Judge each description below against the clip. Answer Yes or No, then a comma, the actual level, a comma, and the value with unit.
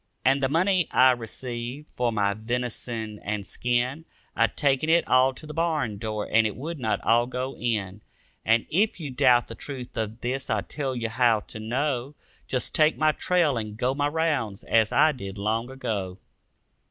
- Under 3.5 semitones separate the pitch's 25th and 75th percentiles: No, average, 4.5 semitones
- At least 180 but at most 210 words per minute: Yes, average, 185 wpm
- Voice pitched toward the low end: Yes, low, 125 Hz